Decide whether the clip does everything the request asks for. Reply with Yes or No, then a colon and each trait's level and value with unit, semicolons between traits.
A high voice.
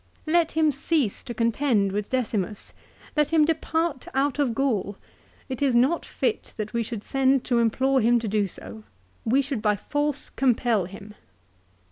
Yes: very high, 250 Hz